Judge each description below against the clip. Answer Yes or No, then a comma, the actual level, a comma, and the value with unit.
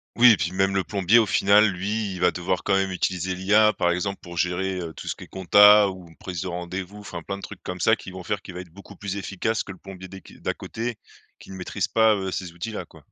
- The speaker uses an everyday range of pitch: No, narrow, 2.2 semitones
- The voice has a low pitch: Yes, very low, 95 Hz